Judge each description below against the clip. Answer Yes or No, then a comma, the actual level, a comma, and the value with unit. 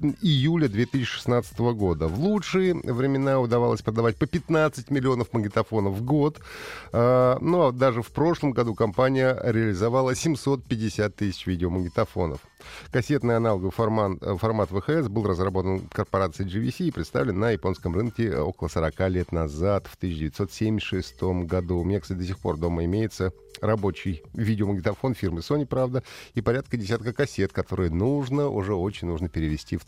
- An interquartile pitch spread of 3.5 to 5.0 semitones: No, wide, 5.5 semitones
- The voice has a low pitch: Yes, low, 110 Hz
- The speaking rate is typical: Yes, average, 145 wpm